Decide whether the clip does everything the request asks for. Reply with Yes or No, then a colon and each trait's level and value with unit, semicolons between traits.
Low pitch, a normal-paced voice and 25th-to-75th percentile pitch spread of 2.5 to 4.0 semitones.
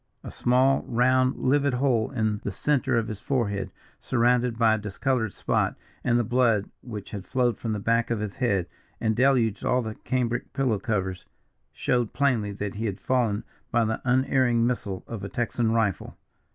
Yes: low, 115 Hz; average, 180 wpm; average, 3.0 semitones